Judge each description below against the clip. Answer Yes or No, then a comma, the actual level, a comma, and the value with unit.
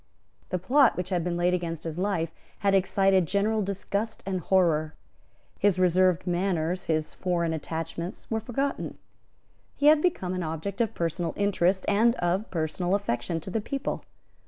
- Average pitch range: Yes, average, 3.1 semitones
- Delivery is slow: No, average, 155 wpm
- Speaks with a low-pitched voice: No, medium, 185 Hz